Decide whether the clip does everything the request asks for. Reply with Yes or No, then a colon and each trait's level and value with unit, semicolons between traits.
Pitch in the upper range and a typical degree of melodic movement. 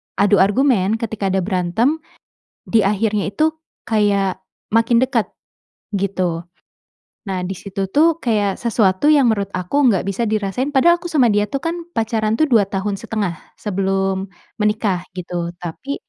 Yes: high, 205 Hz; average, 3.6 semitones